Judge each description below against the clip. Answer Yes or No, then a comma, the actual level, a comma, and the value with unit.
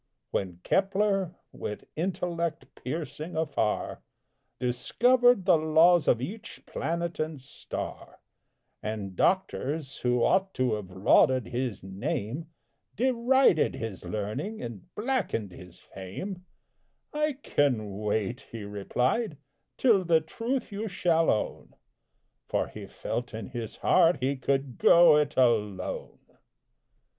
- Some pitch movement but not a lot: No, wide, 9.0 semitones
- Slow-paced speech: Yes, slow, 115 wpm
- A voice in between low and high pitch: Yes, medium, 150 Hz